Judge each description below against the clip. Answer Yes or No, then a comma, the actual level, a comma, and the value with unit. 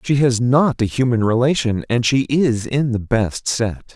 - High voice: No, low, 125 Hz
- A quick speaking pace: No, average, 195 wpm